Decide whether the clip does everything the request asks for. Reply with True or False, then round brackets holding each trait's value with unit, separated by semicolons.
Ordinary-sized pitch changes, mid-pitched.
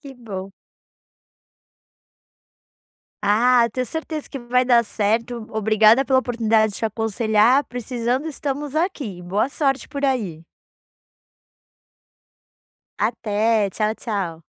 False (3.4 semitones; 230 Hz)